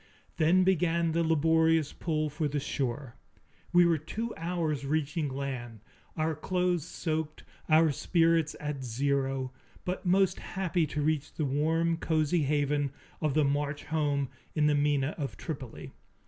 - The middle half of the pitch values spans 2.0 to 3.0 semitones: Yes, narrow, 2.6 semitones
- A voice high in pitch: No, medium, 155 Hz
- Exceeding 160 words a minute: No, average, 145 wpm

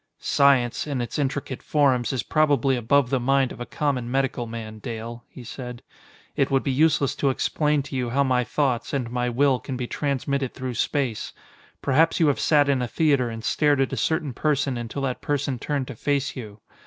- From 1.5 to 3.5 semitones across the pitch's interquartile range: Yes, narrow, 2.6 semitones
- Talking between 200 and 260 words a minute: Yes, fast, 205 wpm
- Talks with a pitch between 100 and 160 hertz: Yes, low, 135 Hz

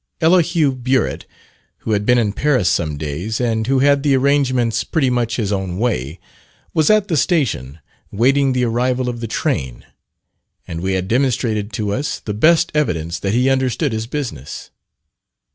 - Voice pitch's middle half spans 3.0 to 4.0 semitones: No, average, 5.2 semitones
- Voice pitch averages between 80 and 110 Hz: No, low, 120 Hz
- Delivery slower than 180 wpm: Yes, average, 170 wpm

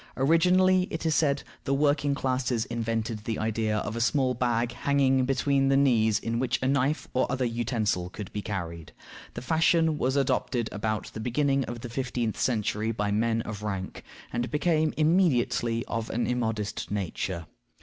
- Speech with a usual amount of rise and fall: Yes, average, 3.9 semitones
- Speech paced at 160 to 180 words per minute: Yes, average, 170 wpm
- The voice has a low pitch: Yes, low, 120 Hz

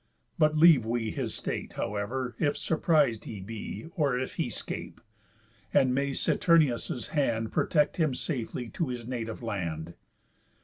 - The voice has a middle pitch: No, low, 125 Hz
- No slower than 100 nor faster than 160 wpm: Yes, average, 140 wpm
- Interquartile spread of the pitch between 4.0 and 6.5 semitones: Yes, average, 4.8 semitones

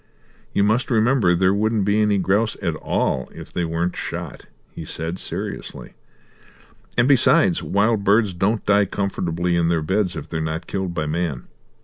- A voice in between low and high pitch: No, very low, 95 Hz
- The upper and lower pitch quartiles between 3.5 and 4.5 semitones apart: Yes, average, 4.0 semitones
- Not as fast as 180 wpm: Yes, average, 165 wpm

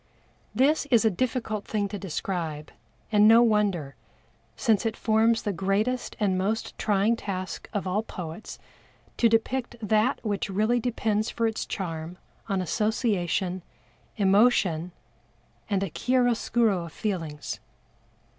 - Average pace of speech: No, slow, 130 wpm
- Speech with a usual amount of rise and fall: Yes, average, 3.3 semitones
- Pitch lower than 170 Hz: No, high, 210 Hz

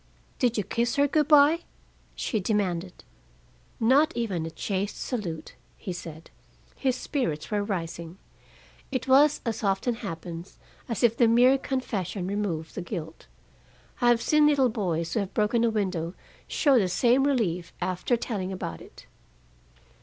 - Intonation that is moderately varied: No, wide, 5.8 semitones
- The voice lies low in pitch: No, high, 210 Hz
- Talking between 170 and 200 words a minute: No, average, 150 wpm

